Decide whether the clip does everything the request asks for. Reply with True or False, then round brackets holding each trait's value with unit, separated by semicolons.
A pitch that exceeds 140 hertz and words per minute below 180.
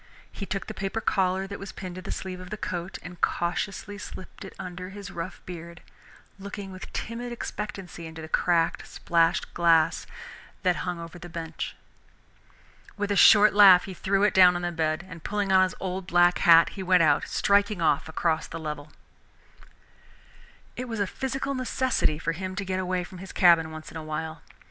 False (185 Hz; 190 wpm)